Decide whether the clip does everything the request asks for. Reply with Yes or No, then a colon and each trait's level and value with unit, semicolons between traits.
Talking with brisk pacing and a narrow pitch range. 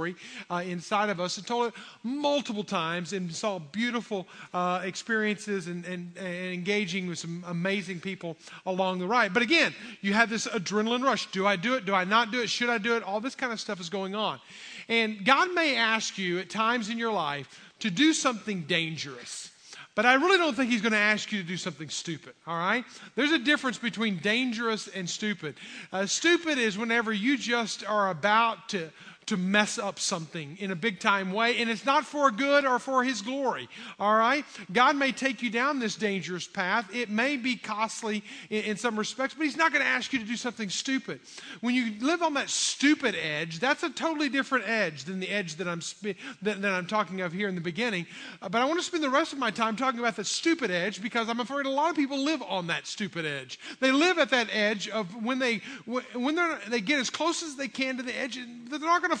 No: fast, 230 wpm; average, 5.2 semitones